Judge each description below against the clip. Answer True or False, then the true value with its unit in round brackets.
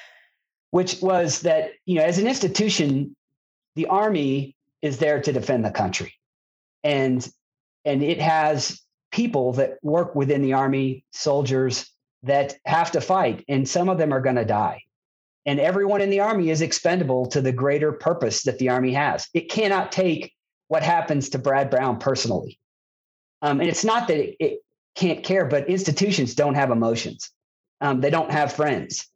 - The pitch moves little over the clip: False (4.9 semitones)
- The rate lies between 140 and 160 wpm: False (170 wpm)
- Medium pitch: True (150 Hz)